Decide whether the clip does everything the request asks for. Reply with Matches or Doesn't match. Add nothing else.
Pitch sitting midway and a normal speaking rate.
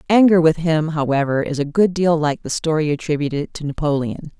Matches